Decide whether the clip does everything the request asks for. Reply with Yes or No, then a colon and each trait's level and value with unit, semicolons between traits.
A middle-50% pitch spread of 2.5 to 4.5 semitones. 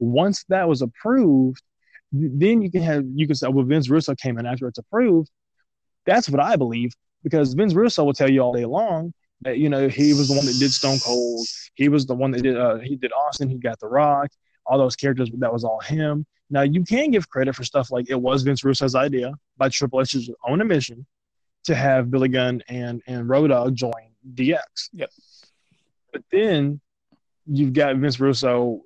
Yes: average, 2.8 semitones